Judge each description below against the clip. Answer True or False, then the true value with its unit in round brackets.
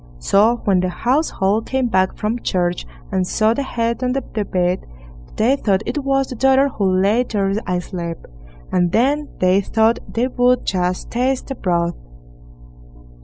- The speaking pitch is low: False (220 Hz)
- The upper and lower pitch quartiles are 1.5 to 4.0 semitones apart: False (5.3 semitones)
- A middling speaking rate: True (160 wpm)